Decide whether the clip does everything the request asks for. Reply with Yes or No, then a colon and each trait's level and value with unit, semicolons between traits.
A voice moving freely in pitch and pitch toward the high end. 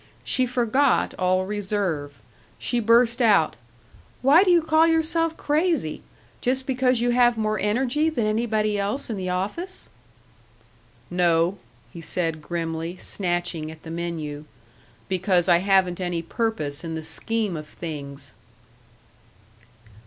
Yes: wide, 6.4 semitones; high, 200 Hz